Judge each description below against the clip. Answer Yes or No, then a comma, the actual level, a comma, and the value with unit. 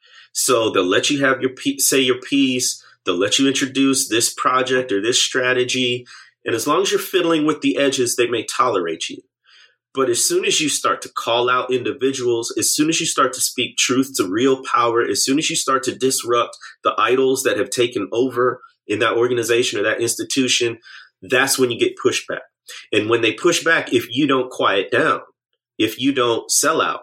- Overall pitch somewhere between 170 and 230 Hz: No, low, 135 Hz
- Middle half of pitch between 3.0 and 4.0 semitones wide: No, wide, 5.6 semitones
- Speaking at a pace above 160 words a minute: Yes, average, 200 wpm